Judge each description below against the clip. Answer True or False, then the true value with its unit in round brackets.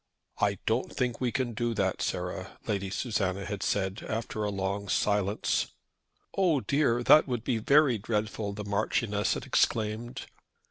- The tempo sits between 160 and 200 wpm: False (150 wpm)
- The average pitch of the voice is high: False (110 Hz)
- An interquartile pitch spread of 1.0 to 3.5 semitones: True (3.1 semitones)